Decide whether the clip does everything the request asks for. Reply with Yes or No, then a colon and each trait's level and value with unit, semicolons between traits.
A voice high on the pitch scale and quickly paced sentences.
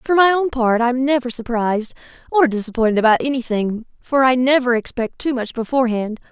No: high, 245 Hz; average, 180 wpm